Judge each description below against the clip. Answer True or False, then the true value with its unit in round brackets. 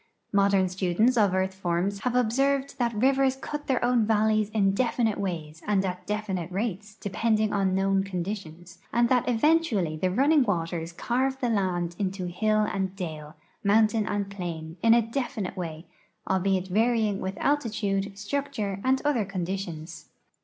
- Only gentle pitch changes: False (3.9 semitones)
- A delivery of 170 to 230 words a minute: False (160 wpm)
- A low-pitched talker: False (200 Hz)